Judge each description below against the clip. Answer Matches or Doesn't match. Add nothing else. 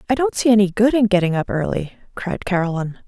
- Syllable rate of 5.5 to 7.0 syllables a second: Matches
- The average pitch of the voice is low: Doesn't match